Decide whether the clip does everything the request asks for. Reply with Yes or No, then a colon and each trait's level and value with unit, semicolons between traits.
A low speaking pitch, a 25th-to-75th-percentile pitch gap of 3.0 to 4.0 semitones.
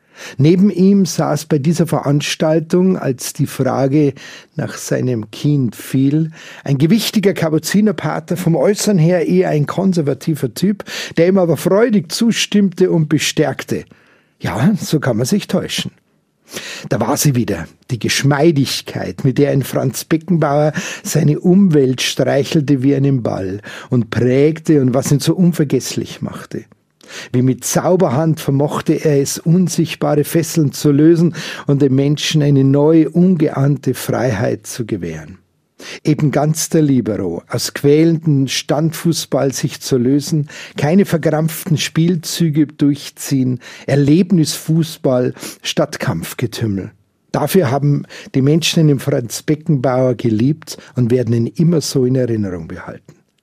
No: medium, 150 Hz; average, 3.7 semitones